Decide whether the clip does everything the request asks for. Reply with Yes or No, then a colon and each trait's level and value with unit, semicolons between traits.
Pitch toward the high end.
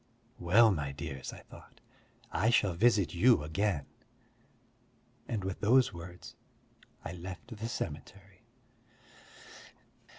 No: very low, 95 Hz